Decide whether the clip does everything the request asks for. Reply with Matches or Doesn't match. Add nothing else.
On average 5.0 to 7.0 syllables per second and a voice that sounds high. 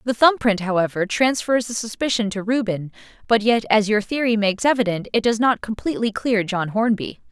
Matches